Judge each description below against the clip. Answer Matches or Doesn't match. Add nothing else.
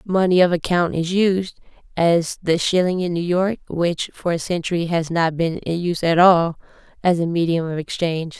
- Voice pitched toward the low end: Doesn't match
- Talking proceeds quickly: Doesn't match